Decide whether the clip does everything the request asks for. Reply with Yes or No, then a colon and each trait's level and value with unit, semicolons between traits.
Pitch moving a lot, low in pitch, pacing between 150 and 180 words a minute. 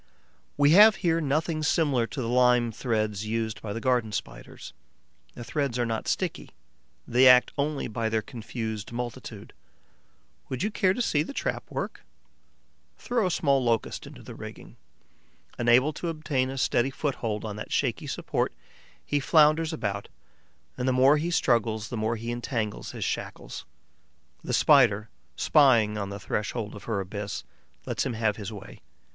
No: average, 4.8 semitones; low, 120 Hz; average, 165 wpm